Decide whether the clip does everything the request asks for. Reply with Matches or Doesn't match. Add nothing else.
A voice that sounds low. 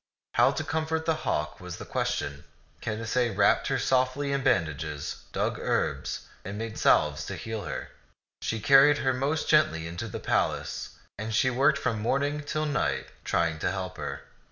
Matches